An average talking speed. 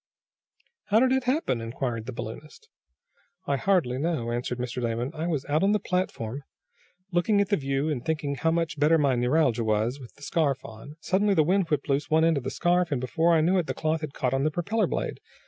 No: fast, 225 wpm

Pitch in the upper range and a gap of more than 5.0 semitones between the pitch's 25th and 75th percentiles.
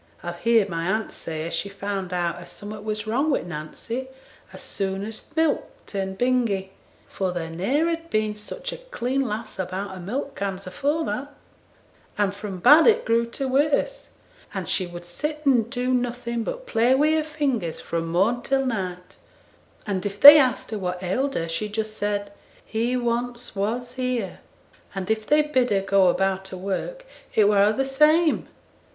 Yes: high, 220 Hz; wide, 5.6 semitones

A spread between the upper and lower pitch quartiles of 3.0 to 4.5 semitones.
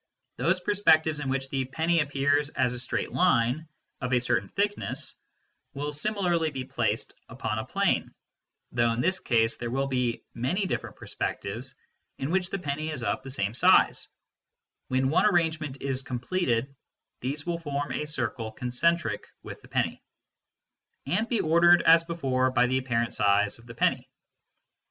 No: average, 5.0 semitones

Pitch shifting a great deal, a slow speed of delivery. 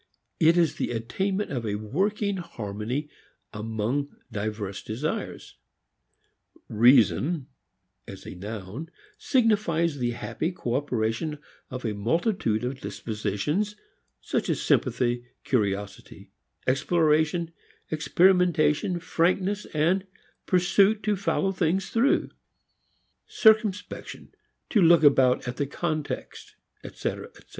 Yes: wide, 8.0 semitones; slow, 100 wpm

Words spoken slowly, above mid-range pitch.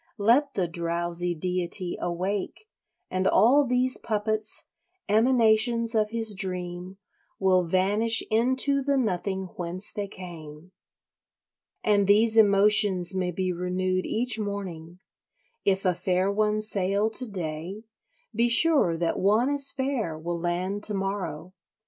Yes: slow, 125 wpm; high, 195 Hz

